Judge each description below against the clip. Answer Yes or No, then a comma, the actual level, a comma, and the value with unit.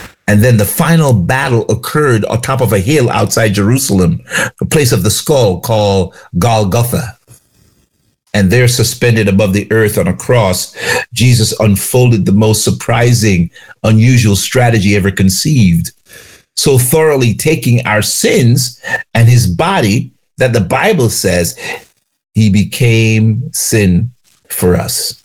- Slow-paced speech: Yes, slow, 130 wpm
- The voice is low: Yes, low, 110 Hz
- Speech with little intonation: No, average, 3.3 semitones